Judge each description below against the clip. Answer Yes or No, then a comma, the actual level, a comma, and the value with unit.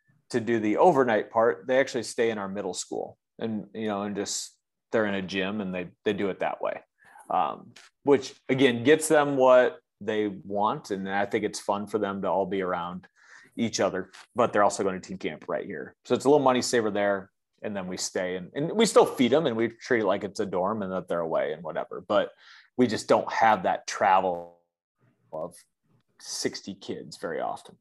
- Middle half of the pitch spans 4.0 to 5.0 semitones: Yes, average, 4.5 semitones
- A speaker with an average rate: No, fast, 220 wpm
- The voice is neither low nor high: No, low, 105 Hz